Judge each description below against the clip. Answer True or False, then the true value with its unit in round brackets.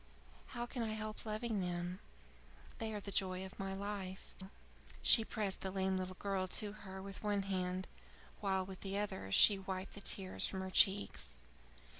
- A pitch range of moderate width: False (1.8 semitones)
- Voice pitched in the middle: False (195 Hz)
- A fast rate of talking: False (175 wpm)